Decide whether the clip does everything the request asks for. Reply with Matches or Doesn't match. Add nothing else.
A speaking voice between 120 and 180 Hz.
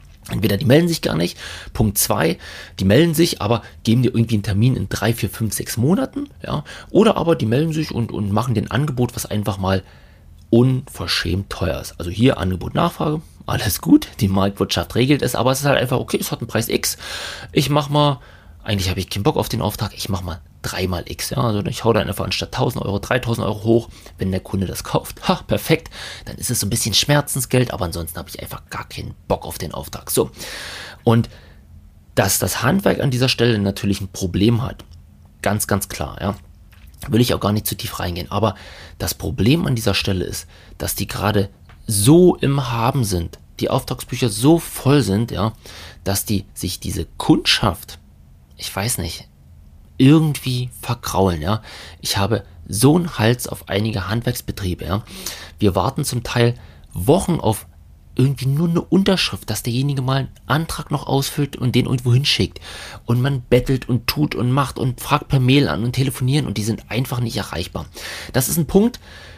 Doesn't match